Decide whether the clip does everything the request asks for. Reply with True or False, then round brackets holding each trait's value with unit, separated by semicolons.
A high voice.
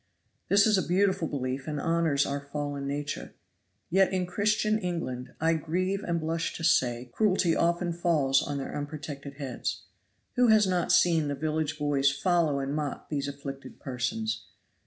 False (155 Hz)